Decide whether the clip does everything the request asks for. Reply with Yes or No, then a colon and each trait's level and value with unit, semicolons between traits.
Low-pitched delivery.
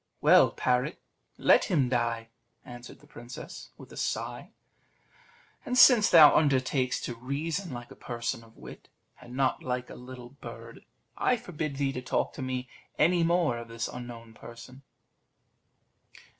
Yes: low, 130 Hz